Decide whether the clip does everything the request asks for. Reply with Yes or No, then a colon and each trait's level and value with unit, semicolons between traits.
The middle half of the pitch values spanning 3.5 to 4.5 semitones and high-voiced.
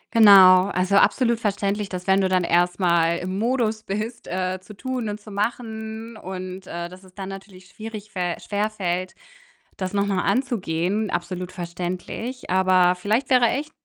No: average, 3.1 semitones; high, 195 Hz